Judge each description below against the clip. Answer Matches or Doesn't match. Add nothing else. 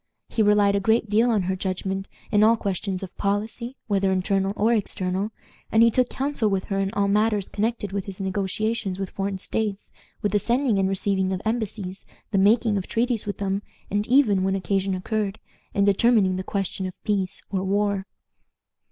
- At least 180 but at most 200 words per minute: Matches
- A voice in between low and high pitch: Doesn't match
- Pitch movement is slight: Matches